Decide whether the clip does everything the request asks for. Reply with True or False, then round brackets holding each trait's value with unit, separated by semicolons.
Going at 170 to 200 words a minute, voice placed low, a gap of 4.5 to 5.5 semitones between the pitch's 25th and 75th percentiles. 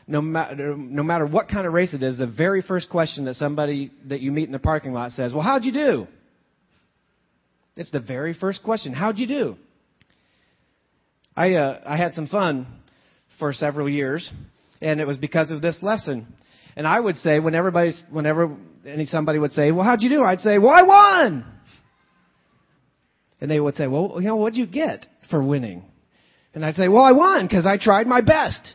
False (195 wpm; 160 Hz; 5.2 semitones)